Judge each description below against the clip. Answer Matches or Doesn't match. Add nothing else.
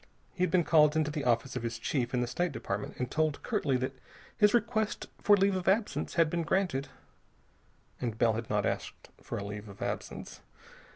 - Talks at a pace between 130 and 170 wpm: Doesn't match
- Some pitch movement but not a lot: Doesn't match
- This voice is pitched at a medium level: Matches